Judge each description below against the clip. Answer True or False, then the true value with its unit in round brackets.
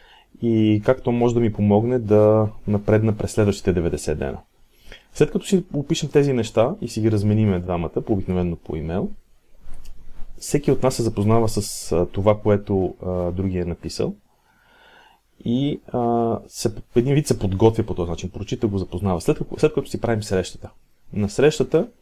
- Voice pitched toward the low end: True (110 Hz)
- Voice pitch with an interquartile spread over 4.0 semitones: True (4.7 semitones)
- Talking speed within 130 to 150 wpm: False (165 wpm)